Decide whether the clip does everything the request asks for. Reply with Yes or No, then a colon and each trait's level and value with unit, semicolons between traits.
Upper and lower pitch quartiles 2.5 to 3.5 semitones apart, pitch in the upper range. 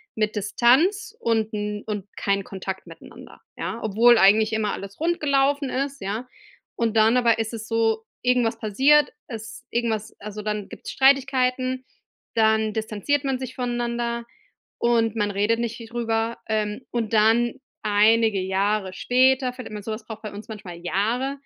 Yes: average, 2.8 semitones; high, 225 Hz